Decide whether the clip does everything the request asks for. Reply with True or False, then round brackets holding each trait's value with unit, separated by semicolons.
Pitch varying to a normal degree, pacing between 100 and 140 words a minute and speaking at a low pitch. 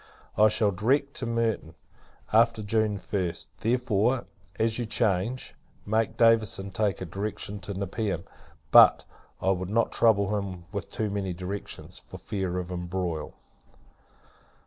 True (3.2 semitones; 135 wpm; 100 Hz)